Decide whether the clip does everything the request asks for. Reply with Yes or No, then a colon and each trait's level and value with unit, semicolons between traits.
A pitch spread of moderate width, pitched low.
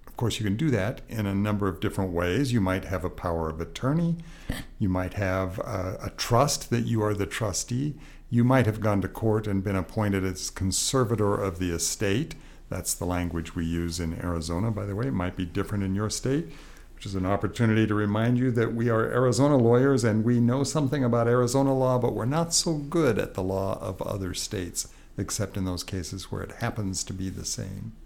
Yes: average, 4.7 semitones; low, 105 Hz